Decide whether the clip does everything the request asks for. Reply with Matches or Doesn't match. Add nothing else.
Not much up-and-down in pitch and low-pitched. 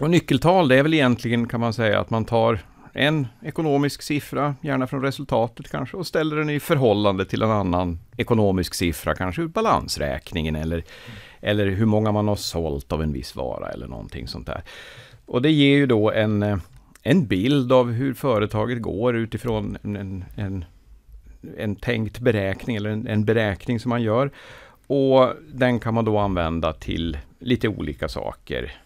Doesn't match